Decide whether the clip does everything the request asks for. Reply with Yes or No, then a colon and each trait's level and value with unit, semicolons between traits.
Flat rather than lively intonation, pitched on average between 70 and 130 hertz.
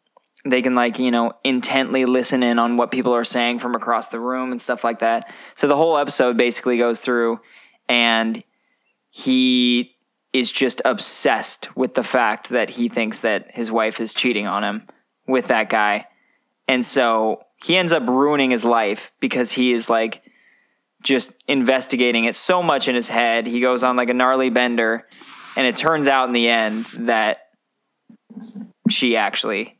Yes: narrow, 1.8 semitones; low, 125 Hz